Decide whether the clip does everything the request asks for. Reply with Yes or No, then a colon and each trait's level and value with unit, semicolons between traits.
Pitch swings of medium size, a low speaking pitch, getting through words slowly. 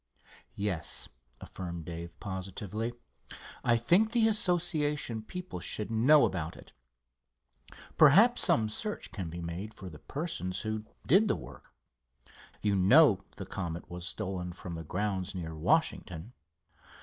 No: wide, 9.0 semitones; low, 105 Hz; slow, 130 wpm